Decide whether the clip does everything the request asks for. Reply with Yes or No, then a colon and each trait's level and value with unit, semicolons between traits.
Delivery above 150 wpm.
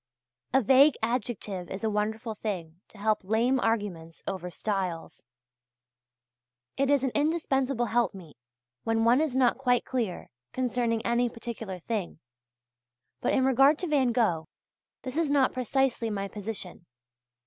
No: slow, 135 wpm